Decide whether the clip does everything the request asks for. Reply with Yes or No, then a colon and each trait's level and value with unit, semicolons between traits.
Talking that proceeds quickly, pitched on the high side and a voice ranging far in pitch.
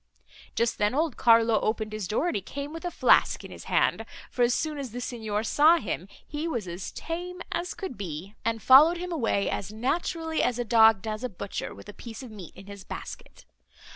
Yes: fast, 220 wpm; high, 235 Hz; wide, 6.6 semitones